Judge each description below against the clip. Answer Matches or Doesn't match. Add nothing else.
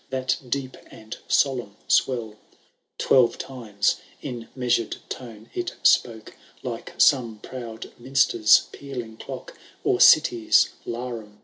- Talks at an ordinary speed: Doesn't match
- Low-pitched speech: Matches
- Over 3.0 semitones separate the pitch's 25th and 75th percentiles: Doesn't match